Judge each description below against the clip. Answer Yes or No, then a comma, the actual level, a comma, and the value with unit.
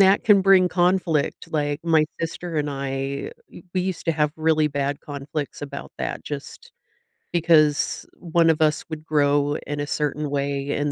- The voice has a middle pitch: Yes, medium, 150 Hz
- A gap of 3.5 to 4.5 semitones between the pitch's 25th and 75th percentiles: No, narrow, 2.6 semitones